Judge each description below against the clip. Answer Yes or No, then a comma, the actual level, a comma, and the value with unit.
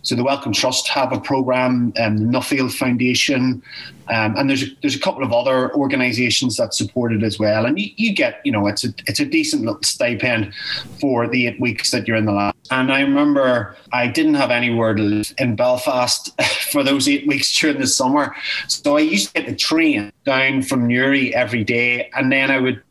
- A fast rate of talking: Yes, fast, 215 wpm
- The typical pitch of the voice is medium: No, low, 125 Hz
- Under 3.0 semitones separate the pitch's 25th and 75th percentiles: Yes, narrow, 2.6 semitones